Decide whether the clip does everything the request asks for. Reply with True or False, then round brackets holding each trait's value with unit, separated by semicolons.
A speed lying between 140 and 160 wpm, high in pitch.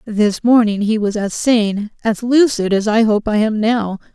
False (205 wpm; 220 Hz)